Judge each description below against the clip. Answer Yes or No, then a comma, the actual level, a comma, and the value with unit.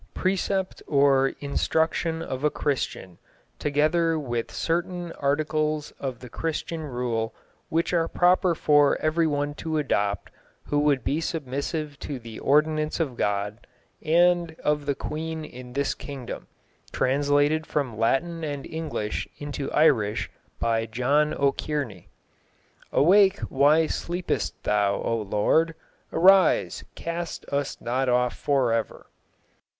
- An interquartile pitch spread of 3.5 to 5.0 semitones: Yes, average, 4.0 semitones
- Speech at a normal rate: No, slow, 120 wpm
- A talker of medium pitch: Yes, medium, 145 Hz